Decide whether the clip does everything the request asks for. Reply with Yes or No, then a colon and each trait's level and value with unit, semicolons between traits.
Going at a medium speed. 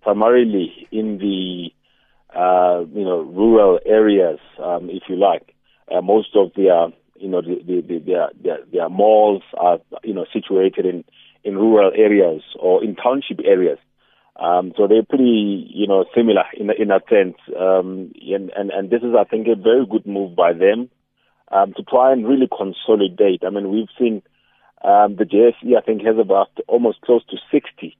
Yes: average, 175 wpm